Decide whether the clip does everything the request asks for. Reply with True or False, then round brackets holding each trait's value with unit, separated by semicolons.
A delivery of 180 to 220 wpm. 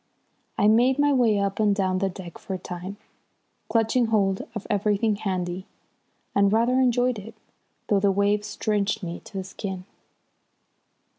False (155 wpm)